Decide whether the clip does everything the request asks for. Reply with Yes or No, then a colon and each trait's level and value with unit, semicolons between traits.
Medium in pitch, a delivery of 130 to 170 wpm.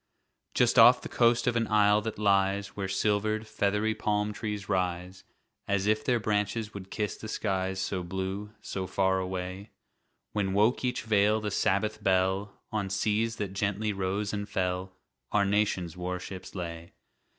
No: low, 100 Hz; average, 160 wpm